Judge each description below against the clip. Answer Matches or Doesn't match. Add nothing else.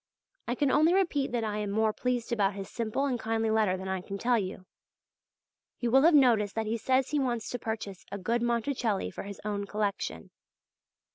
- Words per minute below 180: Doesn't match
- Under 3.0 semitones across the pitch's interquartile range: Doesn't match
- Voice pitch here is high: Matches